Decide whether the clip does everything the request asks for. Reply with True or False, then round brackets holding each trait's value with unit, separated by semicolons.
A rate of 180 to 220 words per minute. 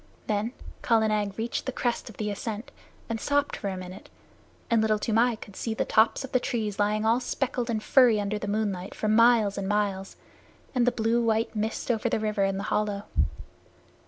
True (200 wpm)